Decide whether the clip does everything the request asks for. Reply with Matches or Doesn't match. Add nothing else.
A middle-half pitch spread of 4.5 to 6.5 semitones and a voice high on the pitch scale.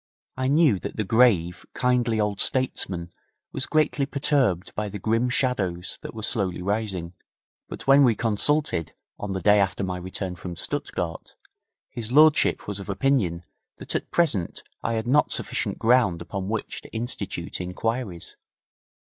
Doesn't match